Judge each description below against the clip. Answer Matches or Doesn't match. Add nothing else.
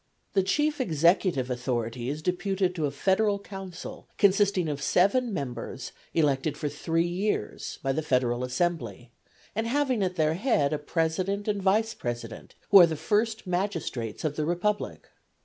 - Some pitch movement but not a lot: Doesn't match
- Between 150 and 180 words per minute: Matches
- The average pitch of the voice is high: Doesn't match